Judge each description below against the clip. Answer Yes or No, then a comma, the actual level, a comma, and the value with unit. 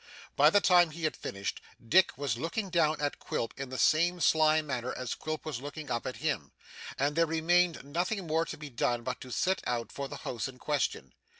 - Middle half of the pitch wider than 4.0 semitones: Yes, average, 4.4 semitones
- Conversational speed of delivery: No, fast, 215 wpm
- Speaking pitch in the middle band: Yes, medium, 155 Hz